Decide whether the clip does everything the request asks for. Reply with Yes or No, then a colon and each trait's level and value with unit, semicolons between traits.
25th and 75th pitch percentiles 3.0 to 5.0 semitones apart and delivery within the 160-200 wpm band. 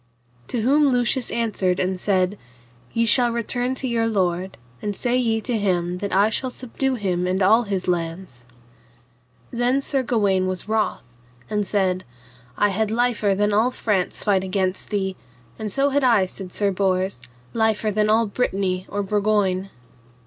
Yes: average, 3.7 semitones; average, 165 wpm